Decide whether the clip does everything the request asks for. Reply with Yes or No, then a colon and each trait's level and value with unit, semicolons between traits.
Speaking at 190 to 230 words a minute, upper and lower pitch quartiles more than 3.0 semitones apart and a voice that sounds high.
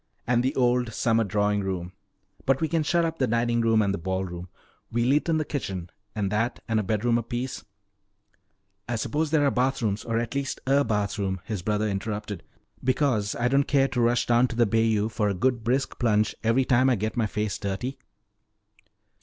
No: fast, 205 wpm; average, 3.8 semitones; low, 115 Hz